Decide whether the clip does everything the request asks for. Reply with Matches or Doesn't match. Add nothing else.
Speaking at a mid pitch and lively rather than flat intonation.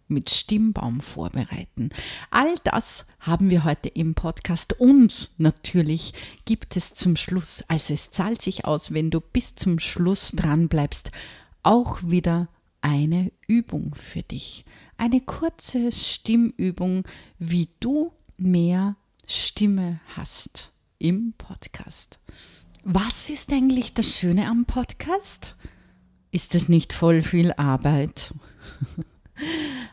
Matches